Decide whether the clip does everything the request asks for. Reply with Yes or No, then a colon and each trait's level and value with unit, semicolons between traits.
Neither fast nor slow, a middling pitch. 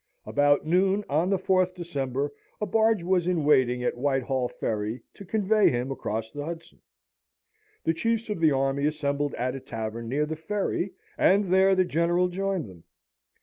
Yes: average, 170 wpm; medium, 160 Hz